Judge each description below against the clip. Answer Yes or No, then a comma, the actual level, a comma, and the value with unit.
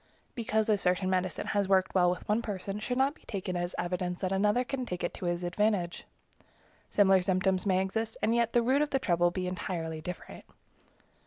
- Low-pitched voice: No, high, 190 Hz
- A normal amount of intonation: Yes, average, 3.3 semitones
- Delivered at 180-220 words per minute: Yes, average, 200 wpm